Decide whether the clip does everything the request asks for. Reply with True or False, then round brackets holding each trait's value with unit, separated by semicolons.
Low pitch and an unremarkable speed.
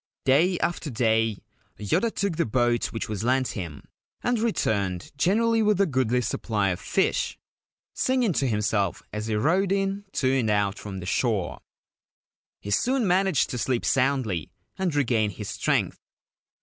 True (125 Hz; 155 wpm)